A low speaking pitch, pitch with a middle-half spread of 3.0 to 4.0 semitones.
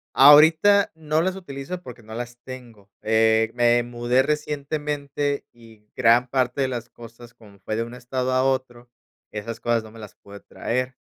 Yes: low, 125 Hz; average, 3.4 semitones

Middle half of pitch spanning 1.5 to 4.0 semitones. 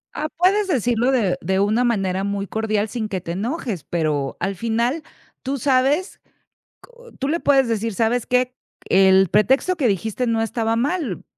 No: average, 5.2 semitones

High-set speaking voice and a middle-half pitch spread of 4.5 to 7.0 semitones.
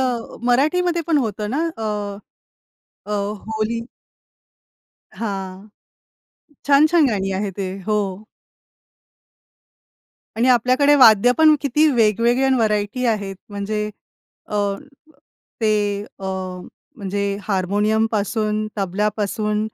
No: high, 215 Hz; average, 3.4 semitones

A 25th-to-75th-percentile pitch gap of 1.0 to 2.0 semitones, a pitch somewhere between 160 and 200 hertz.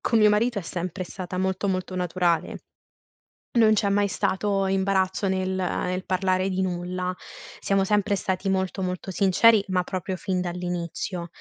Yes: narrow, 1.4 semitones; high, 190 Hz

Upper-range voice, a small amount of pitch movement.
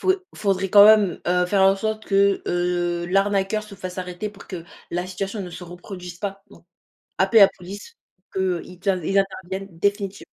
Yes: high, 195 Hz; narrow, 2.0 semitones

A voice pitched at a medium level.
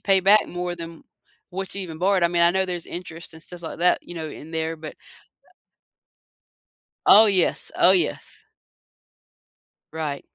Yes: medium, 175 Hz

